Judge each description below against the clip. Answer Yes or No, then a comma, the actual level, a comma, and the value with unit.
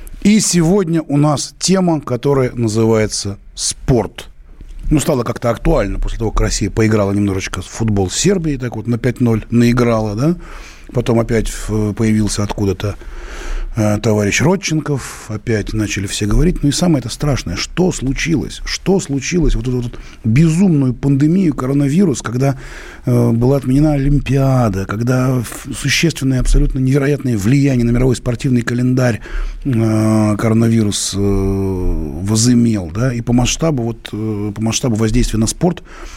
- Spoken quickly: No, average, 140 wpm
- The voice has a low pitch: Yes, low, 120 Hz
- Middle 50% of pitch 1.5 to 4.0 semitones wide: No, average, 4.7 semitones